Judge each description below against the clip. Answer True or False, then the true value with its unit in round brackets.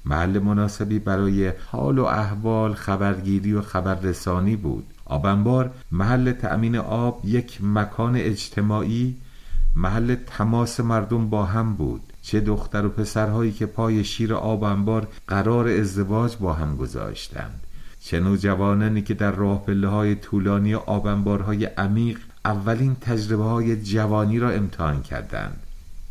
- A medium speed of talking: True (120 wpm)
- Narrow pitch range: True (2.1 semitones)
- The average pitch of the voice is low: True (105 Hz)